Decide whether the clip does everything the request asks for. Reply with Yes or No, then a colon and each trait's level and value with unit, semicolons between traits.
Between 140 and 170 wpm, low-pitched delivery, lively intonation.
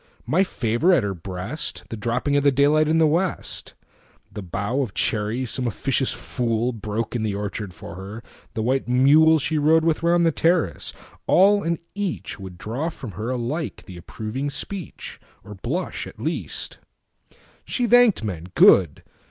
Yes: average, 145 wpm; low, 130 Hz; wide, 6.9 semitones